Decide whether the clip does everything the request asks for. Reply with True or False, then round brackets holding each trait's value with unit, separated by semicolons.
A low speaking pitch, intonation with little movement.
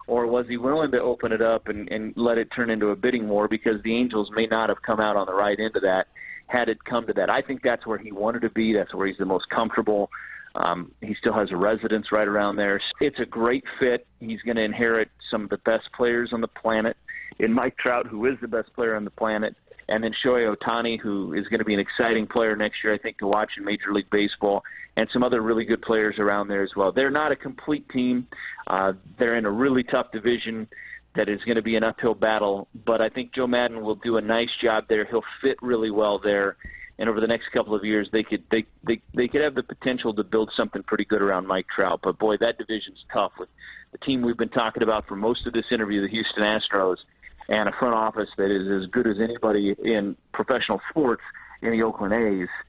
True (110 Hz; 2.1 semitones)